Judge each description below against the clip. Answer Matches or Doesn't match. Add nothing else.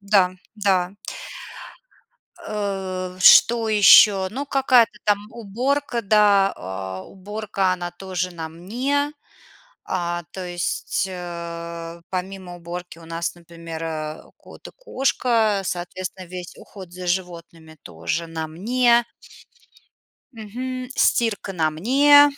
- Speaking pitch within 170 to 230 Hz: Matches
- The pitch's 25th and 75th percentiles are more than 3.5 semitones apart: Matches